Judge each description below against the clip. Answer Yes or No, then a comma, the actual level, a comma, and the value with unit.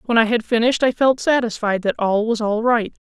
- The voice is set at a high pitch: Yes, high, 230 Hz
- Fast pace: Yes, fast, 235 wpm